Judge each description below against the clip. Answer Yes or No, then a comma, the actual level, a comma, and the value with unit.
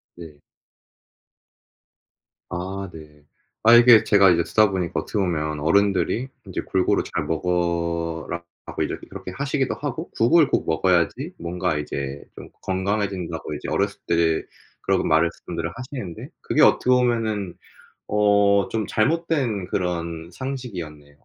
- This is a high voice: No, very low, 90 Hz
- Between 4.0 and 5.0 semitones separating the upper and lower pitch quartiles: Yes, average, 4.5 semitones